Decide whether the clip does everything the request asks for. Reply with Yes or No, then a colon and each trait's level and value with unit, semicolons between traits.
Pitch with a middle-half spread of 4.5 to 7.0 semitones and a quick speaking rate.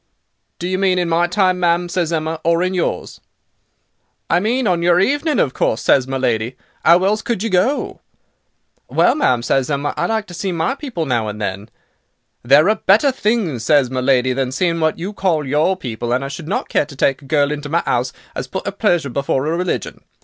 Yes: wide, 5.6 semitones; fast, 215 wpm